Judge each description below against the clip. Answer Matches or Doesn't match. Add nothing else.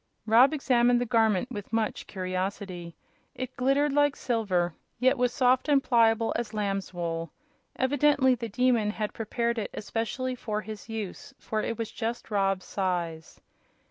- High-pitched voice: Matches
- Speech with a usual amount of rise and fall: Matches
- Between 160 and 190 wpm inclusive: Doesn't match